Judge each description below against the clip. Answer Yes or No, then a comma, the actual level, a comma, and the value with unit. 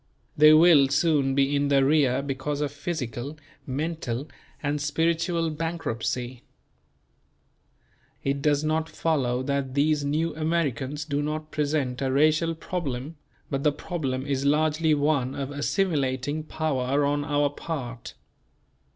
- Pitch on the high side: No, medium, 145 Hz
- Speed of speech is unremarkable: No, slow, 125 wpm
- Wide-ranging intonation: No, narrow, 2.4 semitones